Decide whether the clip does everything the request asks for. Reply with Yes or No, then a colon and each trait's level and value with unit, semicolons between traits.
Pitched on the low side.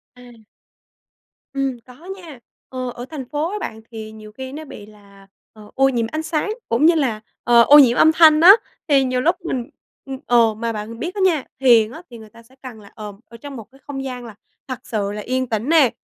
No: very high, 250 Hz